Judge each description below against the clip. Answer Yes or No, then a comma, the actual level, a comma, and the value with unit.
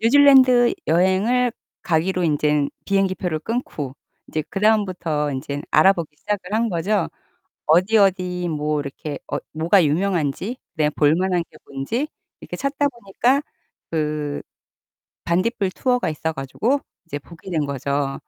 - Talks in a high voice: No, medium, 180 Hz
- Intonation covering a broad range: Yes, wide, 5.8 semitones